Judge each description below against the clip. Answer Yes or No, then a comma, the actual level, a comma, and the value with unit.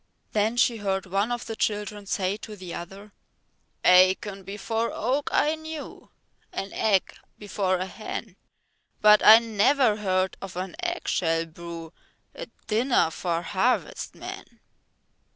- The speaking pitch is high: Yes, high, 205 Hz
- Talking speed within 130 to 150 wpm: Yes, slow, 135 wpm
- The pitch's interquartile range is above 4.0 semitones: No, average, 3.3 semitones